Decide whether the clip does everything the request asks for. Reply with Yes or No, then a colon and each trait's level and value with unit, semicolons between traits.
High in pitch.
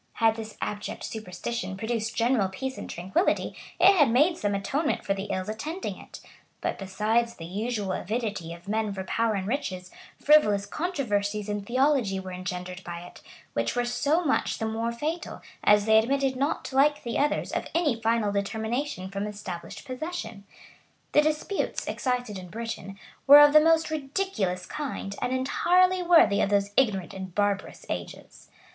Yes: high, 225 Hz